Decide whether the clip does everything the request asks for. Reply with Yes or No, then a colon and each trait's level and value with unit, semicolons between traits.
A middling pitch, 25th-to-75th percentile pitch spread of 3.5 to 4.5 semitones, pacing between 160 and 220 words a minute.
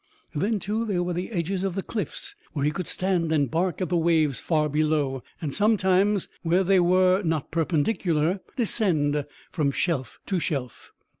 Yes: medium, 175 Hz; average, 3.8 semitones; average, 170 wpm